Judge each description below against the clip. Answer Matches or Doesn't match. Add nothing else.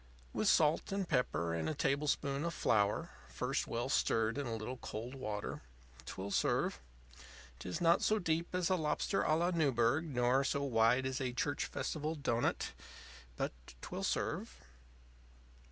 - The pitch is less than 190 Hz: Matches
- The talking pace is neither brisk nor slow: Matches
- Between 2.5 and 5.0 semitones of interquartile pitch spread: Doesn't match